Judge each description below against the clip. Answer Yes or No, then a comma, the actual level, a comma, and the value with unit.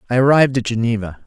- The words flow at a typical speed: Yes, average, 190 wpm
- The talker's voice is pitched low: Yes, low, 120 Hz